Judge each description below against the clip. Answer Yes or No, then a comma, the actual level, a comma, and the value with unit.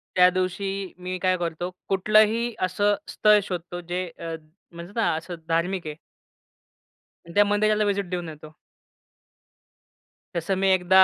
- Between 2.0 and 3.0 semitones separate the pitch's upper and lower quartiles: Yes, narrow, 2.5 semitones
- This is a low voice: No, medium, 185 Hz